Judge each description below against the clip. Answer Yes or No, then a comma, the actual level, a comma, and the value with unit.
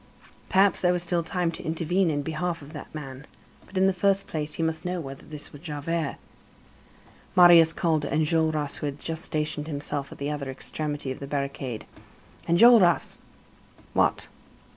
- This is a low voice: No, medium, 160 Hz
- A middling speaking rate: Yes, average, 170 wpm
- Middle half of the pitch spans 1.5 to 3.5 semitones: Yes, average, 3.0 semitones